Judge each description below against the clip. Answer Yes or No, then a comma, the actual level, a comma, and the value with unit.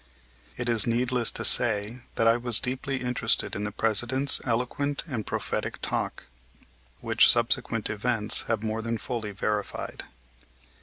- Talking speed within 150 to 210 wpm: No, average, 140 wpm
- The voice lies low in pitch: Yes, low, 115 Hz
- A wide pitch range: No, narrow, 2.6 semitones